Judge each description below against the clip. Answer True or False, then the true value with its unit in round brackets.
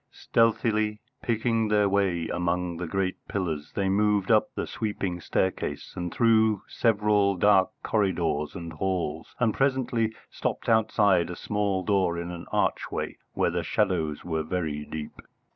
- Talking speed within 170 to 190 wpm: False (145 wpm)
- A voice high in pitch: False (95 Hz)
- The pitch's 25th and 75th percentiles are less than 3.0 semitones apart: False (3.6 semitones)